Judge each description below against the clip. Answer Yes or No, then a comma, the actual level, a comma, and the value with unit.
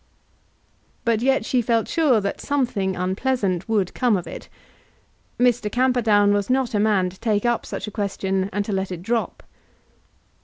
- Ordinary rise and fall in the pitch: Yes, average, 3.9 semitones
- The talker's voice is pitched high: Yes, high, 215 Hz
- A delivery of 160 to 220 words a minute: Yes, average, 165 wpm